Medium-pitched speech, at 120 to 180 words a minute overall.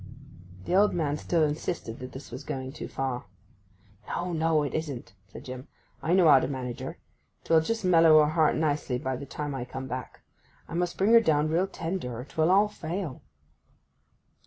No: medium, 155 Hz; average, 190 wpm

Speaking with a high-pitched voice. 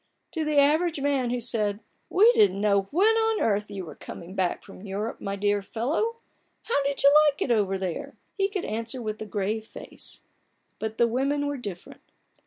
Yes: high, 230 Hz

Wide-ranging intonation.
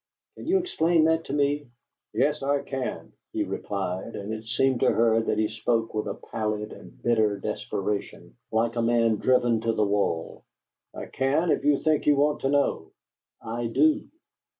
No: average, 4.8 semitones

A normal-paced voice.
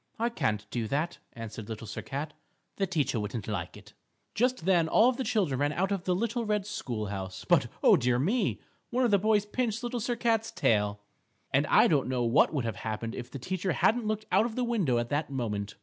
No: fast, 225 wpm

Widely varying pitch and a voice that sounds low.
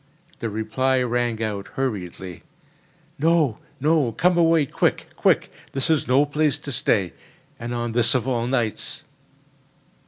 No: average, 4.2 semitones; low, 125 Hz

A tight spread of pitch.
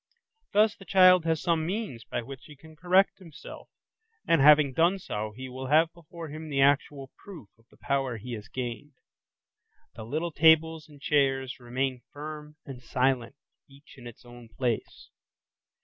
No: average, 4.2 semitones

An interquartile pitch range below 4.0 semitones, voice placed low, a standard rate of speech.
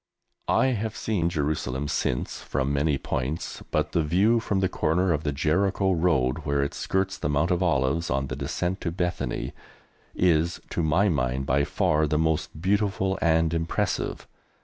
No: average, 4.3 semitones; very low, 80 Hz; average, 170 wpm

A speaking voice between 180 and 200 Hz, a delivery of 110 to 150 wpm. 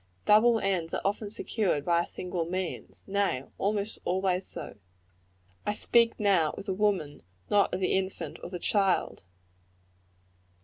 Yes: high, 190 Hz; average, 145 wpm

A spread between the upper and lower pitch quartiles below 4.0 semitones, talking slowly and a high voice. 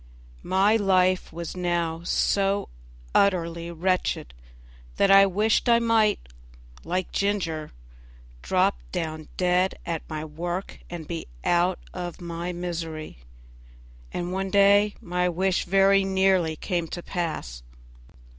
No: narrow, 2.5 semitones; slow, 120 wpm; medium, 180 Hz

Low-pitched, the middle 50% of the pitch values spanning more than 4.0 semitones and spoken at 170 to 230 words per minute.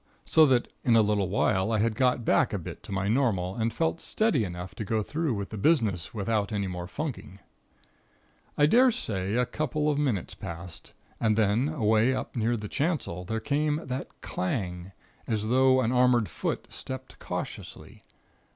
Yes: low, 115 Hz; average, 4.9 semitones; average, 180 wpm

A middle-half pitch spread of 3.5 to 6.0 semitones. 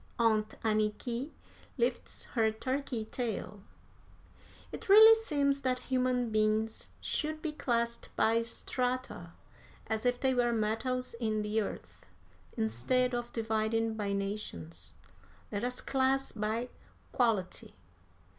No: average, 3.0 semitones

